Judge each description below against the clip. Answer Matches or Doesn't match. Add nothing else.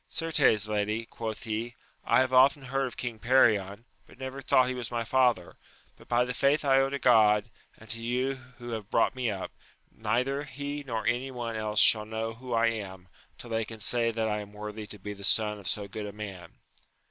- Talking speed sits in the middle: Doesn't match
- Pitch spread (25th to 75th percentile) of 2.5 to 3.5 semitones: Matches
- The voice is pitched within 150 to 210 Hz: Doesn't match